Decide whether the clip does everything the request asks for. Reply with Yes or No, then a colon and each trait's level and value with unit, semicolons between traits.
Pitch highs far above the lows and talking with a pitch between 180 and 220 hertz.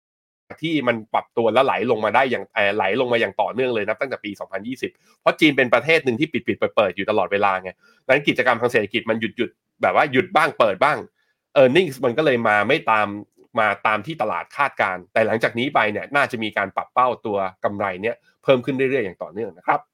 No: wide, 5.9 semitones; low, 115 Hz